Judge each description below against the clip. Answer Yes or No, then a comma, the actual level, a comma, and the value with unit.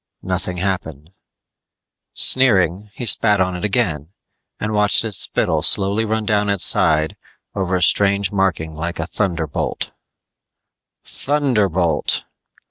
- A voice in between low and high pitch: No, very low, 95 Hz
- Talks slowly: Yes, slow, 120 wpm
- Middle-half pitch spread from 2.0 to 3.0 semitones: No, average, 3.6 semitones